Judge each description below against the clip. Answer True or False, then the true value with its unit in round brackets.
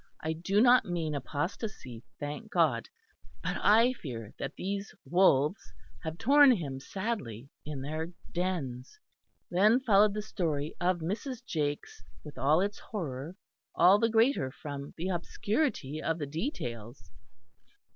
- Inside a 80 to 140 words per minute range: True (135 wpm)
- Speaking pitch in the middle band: True (170 Hz)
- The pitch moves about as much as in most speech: False (6.6 semitones)